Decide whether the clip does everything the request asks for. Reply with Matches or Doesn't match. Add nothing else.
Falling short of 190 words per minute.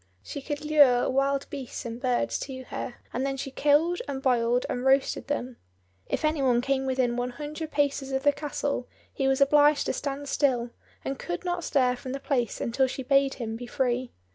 Doesn't match